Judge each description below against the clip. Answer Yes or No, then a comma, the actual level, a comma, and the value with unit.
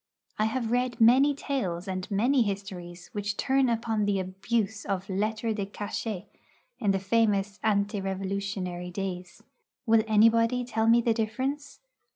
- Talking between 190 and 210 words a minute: No, average, 145 wpm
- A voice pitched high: Yes, high, 210 Hz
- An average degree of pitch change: Yes, average, 3.0 semitones